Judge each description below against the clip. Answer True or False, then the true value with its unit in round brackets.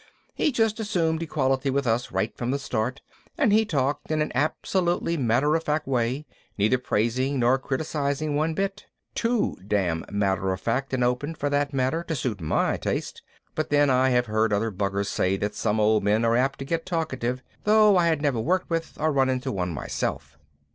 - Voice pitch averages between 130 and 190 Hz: True (135 Hz)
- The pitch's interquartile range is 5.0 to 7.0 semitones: True (5.6 semitones)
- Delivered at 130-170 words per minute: False (195 wpm)